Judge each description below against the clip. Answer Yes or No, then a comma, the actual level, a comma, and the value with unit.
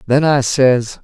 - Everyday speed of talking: Yes, average, 175 wpm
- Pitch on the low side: Yes, low, 130 Hz